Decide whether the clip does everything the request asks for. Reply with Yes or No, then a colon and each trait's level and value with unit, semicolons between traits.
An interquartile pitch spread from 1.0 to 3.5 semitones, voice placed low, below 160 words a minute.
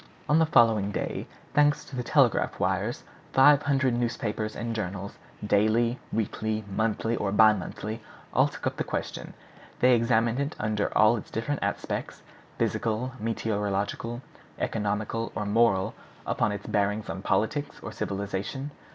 Yes: narrow, 2.5 semitones; low, 110 Hz; average, 145 wpm